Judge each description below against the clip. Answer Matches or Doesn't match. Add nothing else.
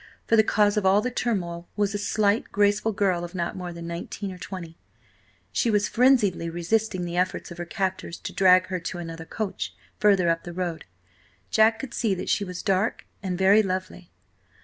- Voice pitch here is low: Doesn't match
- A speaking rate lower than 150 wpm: Doesn't match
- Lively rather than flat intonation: Doesn't match